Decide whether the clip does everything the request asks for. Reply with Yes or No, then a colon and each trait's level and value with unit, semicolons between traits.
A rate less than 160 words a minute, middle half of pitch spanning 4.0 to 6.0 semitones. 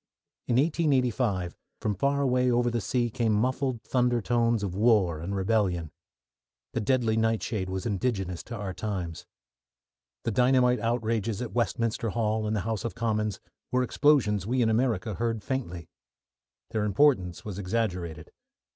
No: average, 145 wpm; average, 3.6 semitones